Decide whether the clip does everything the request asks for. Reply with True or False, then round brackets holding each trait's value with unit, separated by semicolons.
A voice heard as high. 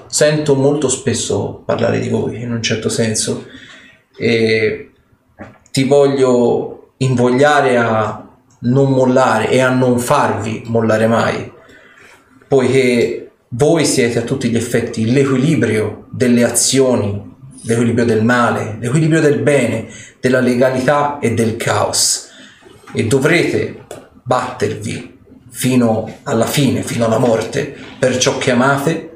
False (125 Hz)